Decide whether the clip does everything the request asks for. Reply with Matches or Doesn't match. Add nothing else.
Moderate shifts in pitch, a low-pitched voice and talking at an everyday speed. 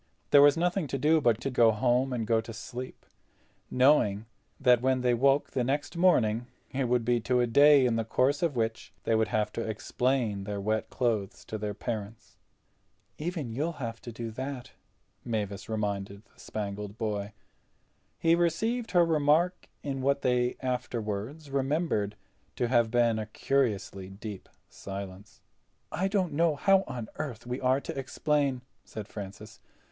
Matches